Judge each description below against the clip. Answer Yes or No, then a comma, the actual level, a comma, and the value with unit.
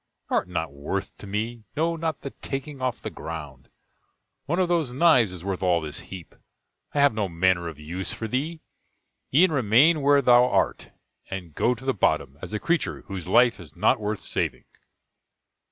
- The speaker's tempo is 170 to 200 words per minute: Yes, average, 185 wpm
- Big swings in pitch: Yes, wide, 7.7 semitones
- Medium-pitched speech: No, low, 110 Hz